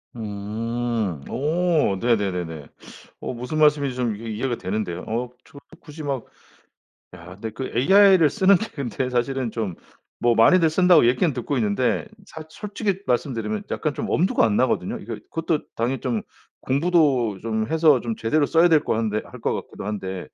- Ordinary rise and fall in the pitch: No, wide, 6.0 semitones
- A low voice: Yes, low, 125 Hz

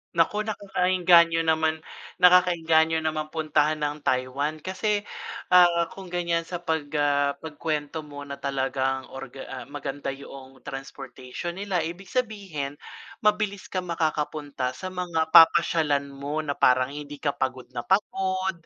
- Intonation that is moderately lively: Yes, average, 3.8 semitones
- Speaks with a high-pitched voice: No, medium, 155 Hz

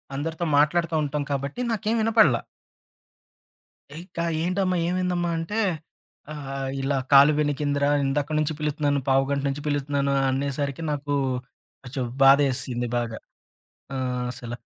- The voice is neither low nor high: Yes, medium, 145 Hz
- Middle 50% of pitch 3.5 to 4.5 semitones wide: No, average, 3.1 semitones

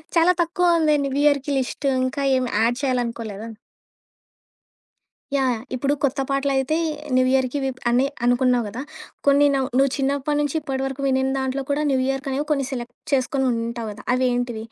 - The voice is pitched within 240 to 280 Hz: Yes, very high, 265 Hz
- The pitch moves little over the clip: Yes, narrow, 2.2 semitones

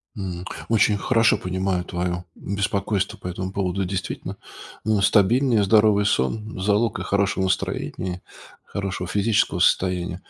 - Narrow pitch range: Yes, narrow, 2.3 semitones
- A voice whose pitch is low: Yes, low, 100 Hz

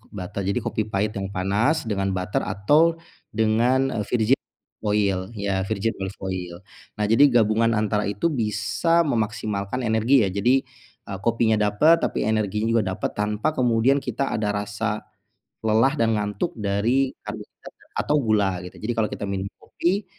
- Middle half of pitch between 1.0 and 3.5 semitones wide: Yes, average, 3.0 semitones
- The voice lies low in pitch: Yes, low, 110 Hz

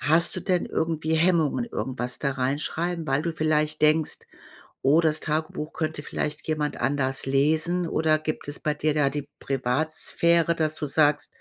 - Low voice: No, medium, 155 Hz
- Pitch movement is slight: Yes, narrow, 1.8 semitones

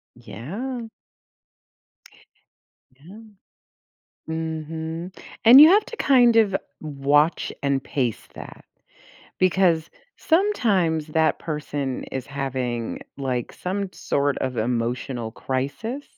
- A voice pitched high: No, medium, 155 Hz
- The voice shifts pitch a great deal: Yes, wide, 6.5 semitones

